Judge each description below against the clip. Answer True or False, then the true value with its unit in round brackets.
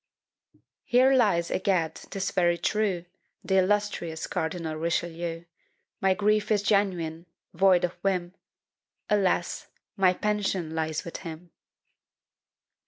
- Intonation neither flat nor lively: True (3.1 semitones)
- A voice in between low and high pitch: True (180 Hz)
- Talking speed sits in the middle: False (105 wpm)